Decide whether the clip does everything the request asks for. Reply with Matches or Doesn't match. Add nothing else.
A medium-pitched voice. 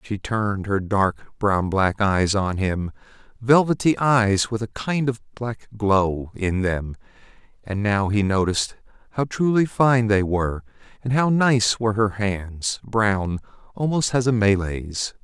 Doesn't match